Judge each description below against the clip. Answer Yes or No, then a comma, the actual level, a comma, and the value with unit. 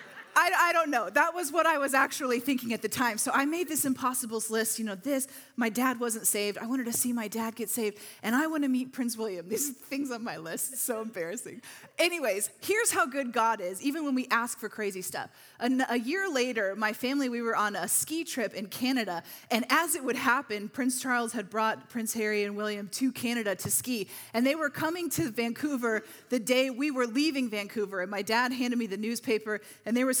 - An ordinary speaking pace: No, fast, 230 wpm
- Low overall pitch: No, high, 245 Hz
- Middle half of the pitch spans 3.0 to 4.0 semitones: Yes, average, 3.7 semitones